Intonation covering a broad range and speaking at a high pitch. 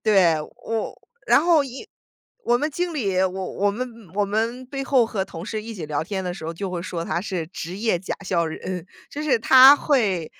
Yes: wide, 5.9 semitones; high, 205 Hz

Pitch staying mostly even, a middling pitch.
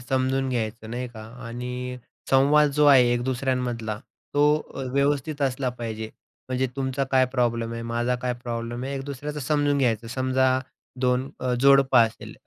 No: narrow, 2.2 semitones; low, 130 Hz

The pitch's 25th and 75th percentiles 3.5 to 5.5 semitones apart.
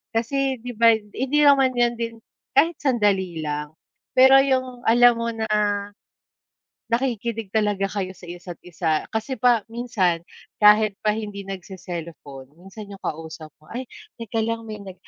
Yes: average, 4.5 semitones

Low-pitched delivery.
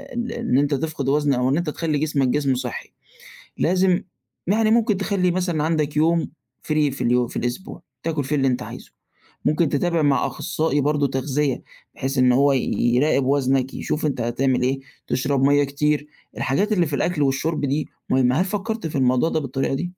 No: medium, 145 Hz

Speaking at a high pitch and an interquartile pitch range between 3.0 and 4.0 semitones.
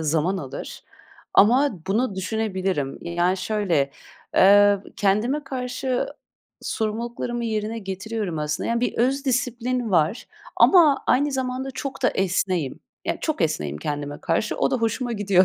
No: high, 215 Hz; wide, 5.4 semitones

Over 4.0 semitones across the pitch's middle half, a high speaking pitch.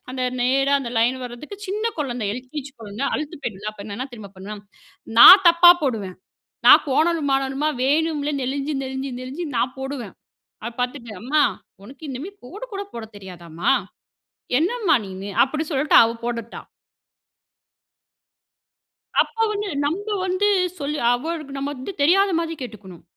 Yes: average, 4.9 semitones; very high, 270 Hz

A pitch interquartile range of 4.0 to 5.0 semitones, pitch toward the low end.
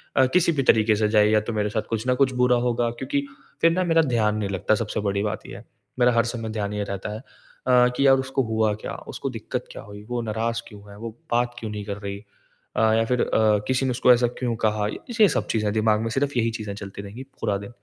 No: average, 2.9 semitones; low, 110 Hz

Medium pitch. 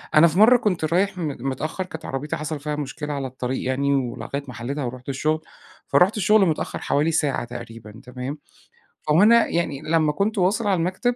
Yes: medium, 150 Hz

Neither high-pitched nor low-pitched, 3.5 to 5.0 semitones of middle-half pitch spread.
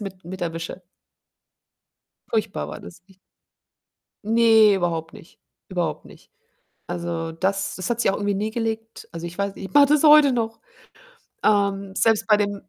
No: high, 200 Hz; average, 4.0 semitones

